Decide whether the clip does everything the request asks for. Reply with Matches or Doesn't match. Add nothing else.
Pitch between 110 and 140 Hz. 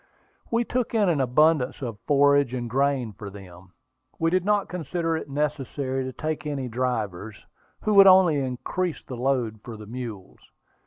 Matches